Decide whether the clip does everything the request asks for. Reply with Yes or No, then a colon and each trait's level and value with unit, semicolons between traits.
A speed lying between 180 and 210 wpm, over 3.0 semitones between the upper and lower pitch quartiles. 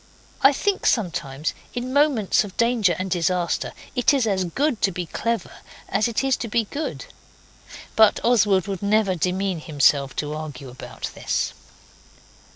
No: average, 155 wpm; wide, 5.4 semitones